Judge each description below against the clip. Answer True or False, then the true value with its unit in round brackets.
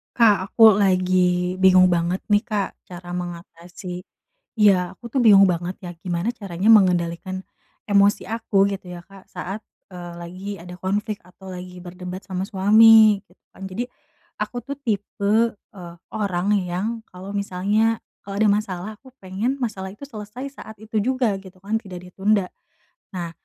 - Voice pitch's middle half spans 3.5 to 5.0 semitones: False (2.7 semitones)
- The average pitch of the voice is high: True (195 Hz)